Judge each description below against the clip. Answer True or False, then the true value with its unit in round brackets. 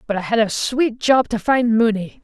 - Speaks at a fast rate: True (240 wpm)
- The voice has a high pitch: True (230 Hz)